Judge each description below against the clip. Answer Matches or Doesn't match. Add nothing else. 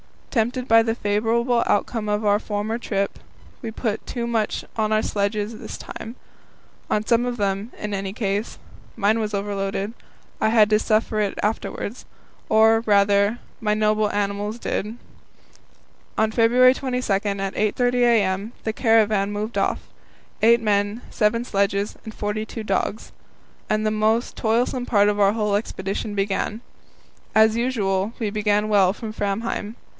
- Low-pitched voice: Doesn't match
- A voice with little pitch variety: Matches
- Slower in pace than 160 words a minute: Matches